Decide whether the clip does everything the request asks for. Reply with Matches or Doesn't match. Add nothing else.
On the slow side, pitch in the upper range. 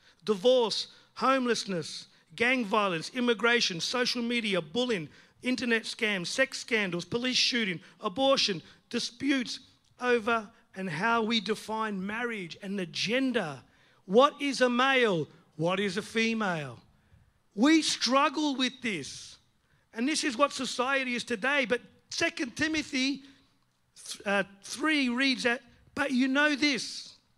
Matches